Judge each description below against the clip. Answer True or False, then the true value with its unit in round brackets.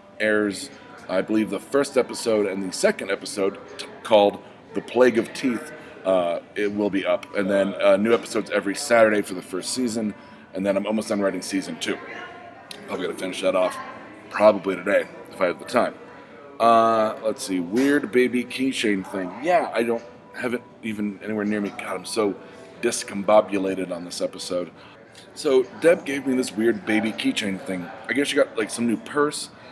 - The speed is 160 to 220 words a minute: True (185 wpm)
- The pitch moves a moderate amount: True (3.3 semitones)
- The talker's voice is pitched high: False (105 Hz)